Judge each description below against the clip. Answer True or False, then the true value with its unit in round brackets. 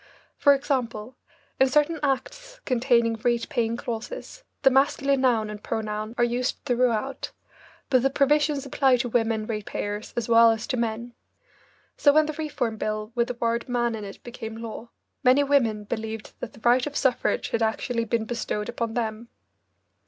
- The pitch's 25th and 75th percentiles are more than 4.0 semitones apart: False (3.2 semitones)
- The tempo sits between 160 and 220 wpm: True (170 wpm)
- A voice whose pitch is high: True (240 Hz)